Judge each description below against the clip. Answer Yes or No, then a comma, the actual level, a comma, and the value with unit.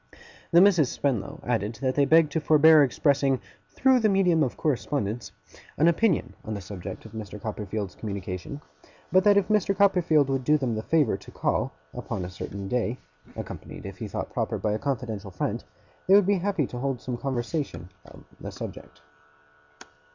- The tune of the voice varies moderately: No, wide, 7.1 semitones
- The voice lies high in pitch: No, low, 135 Hz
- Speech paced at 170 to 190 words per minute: Yes, average, 180 wpm